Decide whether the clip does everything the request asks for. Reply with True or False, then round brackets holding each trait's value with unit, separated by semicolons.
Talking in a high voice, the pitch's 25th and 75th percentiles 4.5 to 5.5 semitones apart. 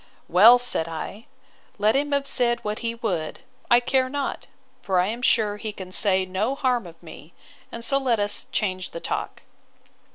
True (215 Hz; 4.9 semitones)